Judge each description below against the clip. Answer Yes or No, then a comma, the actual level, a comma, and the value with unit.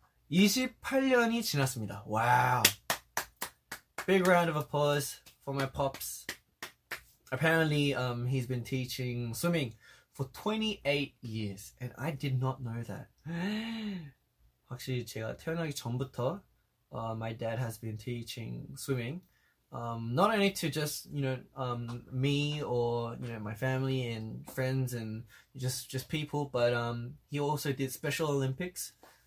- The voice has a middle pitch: No, low, 130 Hz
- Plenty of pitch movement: No, average, 3.9 semitones